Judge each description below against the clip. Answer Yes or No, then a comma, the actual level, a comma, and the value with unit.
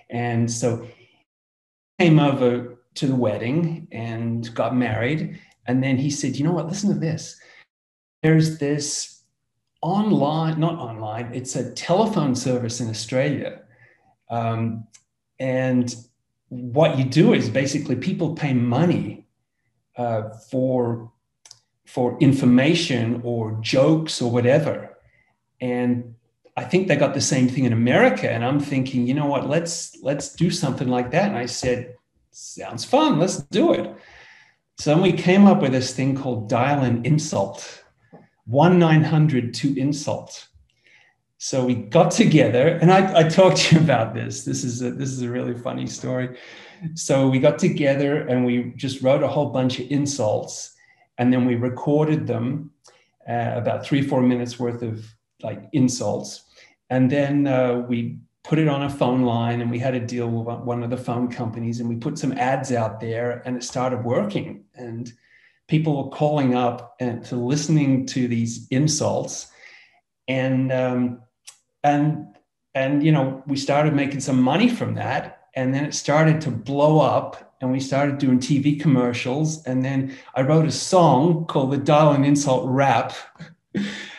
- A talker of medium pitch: No, low, 130 Hz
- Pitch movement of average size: Yes, average, 3.5 semitones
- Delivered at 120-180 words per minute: Yes, average, 160 wpm